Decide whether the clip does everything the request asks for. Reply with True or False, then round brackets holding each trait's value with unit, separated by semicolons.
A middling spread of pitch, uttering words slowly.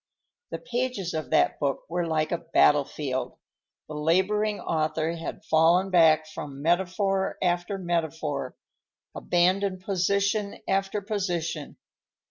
True (3.7 semitones; 110 wpm)